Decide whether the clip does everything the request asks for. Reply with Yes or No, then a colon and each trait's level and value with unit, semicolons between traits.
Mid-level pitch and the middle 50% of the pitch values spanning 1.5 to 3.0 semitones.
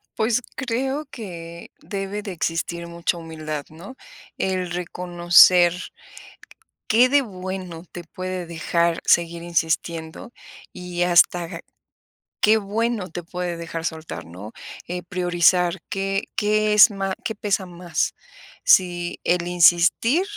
Yes: medium, 180 Hz; narrow, 2.6 semitones